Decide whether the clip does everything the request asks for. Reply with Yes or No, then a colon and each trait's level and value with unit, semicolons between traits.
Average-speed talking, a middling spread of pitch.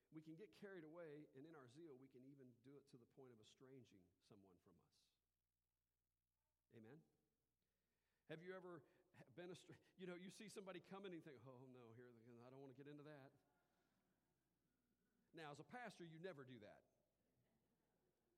No: average, 180 wpm; wide, 6.6 semitones